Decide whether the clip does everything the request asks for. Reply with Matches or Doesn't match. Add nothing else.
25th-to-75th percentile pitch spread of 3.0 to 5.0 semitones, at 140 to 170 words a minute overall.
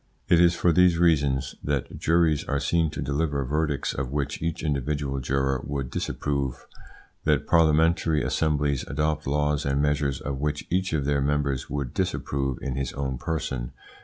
Doesn't match